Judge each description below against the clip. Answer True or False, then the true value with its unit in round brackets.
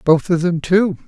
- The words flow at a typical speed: False (225 wpm)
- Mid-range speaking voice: True (170 Hz)